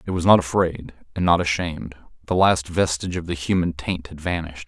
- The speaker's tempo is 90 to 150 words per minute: No, fast, 205 wpm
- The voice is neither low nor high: No, very low, 85 Hz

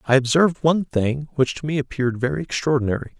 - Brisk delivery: No, average, 190 wpm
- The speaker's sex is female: No, male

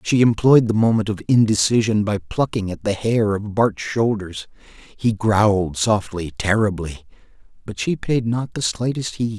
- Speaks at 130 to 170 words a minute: Yes, average, 160 wpm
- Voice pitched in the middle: No, low, 110 Hz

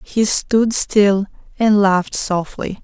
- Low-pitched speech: No, high, 205 Hz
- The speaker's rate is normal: No, slow, 125 wpm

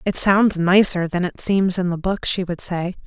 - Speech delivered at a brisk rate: Yes, fast, 235 wpm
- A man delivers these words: No, female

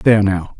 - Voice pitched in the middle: No, low, 100 Hz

